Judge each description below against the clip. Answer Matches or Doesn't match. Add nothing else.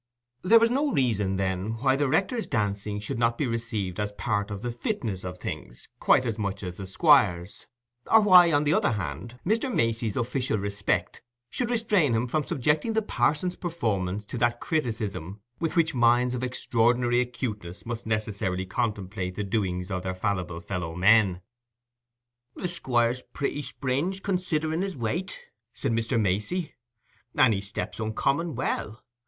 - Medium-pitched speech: Doesn't match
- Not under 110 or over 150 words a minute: Doesn't match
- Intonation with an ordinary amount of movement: Doesn't match